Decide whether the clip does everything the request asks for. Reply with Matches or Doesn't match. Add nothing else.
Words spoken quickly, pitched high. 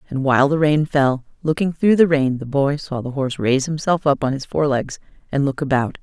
Doesn't match